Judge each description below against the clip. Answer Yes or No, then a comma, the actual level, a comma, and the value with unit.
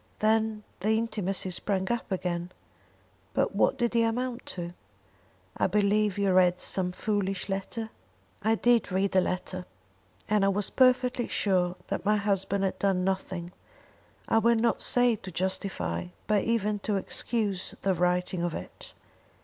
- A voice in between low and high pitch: No, high, 200 Hz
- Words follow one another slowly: No, average, 150 wpm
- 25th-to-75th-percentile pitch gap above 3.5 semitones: No, average, 3.1 semitones